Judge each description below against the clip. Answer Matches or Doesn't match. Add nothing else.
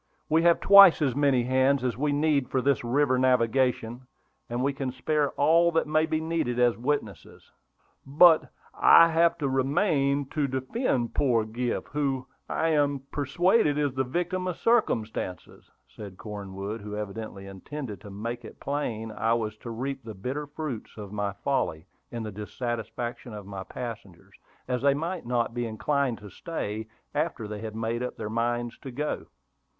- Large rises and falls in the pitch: Doesn't match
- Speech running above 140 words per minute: Matches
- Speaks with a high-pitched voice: Doesn't match